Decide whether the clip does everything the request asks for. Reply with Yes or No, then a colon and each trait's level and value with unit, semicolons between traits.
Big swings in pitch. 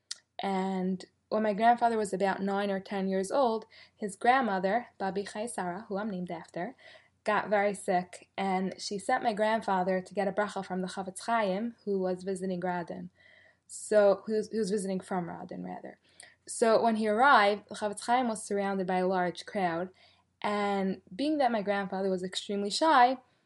No: narrow, 2.4 semitones